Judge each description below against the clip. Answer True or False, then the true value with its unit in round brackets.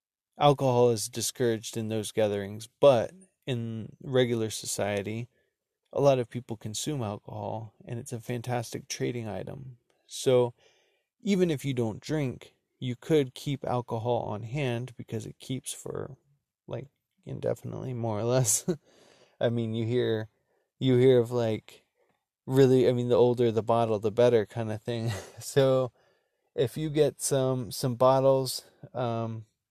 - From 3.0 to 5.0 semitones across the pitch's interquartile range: False (2.5 semitones)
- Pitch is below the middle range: True (120 Hz)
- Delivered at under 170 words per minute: True (145 wpm)